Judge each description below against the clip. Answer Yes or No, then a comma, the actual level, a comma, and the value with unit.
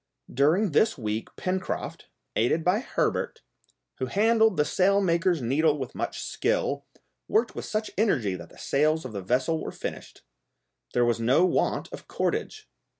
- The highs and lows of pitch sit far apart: Yes, wide, 8.0 semitones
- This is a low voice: No, medium, 160 Hz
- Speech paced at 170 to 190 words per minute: No, average, 155 wpm